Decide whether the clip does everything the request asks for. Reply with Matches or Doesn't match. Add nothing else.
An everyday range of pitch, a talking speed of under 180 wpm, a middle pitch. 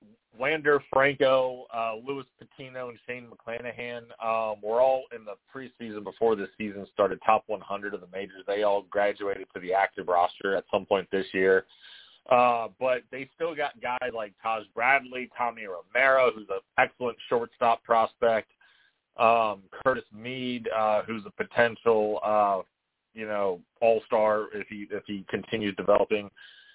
Doesn't match